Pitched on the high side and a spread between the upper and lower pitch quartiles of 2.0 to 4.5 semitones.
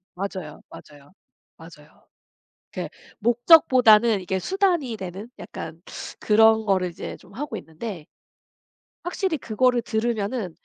No: high, 215 Hz; average, 5.1 semitones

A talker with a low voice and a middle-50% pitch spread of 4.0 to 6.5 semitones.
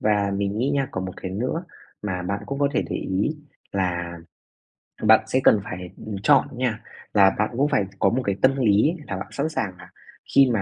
Yes: low, 105 Hz; wide, 5.4 semitones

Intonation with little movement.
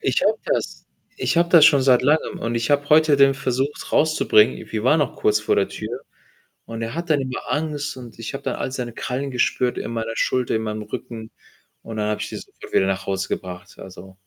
No: average, 4.7 semitones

